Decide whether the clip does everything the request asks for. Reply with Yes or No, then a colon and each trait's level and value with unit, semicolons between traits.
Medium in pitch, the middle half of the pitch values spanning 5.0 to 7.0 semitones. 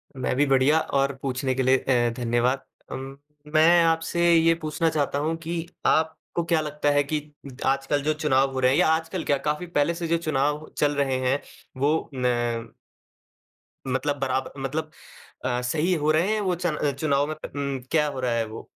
No: medium, 145 Hz; average, 3.3 semitones